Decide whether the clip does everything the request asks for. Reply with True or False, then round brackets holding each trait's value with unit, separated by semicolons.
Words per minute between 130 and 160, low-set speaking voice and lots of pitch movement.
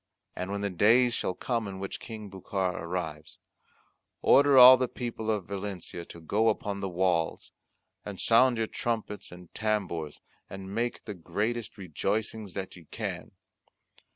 False (155 wpm; 100 Hz; 3.6 semitones)